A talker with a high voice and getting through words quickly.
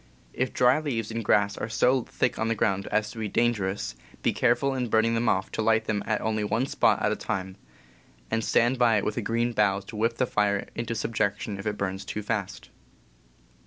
No: low, 110 Hz; fast, 220 wpm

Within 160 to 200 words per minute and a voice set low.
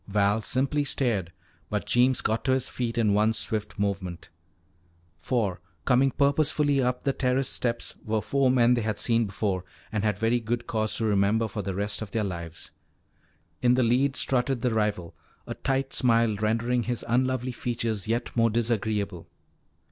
Yes: average, 170 wpm; low, 115 Hz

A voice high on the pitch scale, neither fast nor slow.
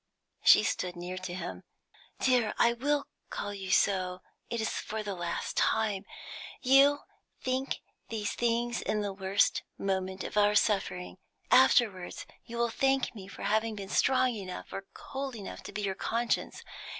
Yes: high, 210 Hz; average, 160 wpm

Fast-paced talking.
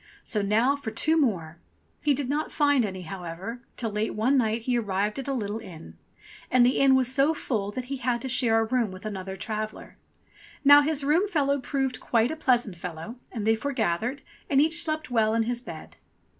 Yes: fast, 210 wpm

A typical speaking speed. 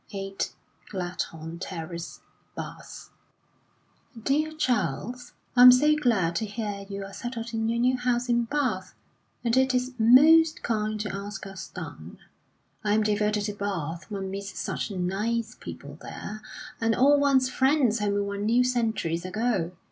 Yes: average, 150 wpm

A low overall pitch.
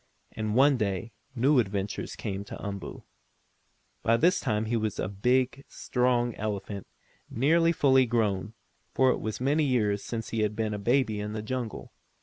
Yes: low, 115 Hz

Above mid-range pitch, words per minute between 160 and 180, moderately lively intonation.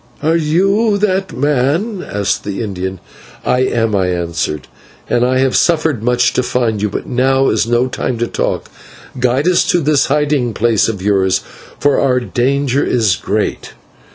No: low, 125 Hz; average, 165 wpm; average, 5.0 semitones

